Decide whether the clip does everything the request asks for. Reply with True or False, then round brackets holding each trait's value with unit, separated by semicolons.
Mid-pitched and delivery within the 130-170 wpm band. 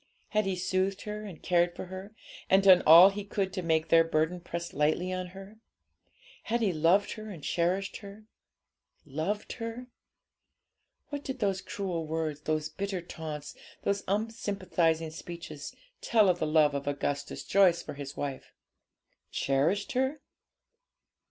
True (180 Hz; 150 wpm)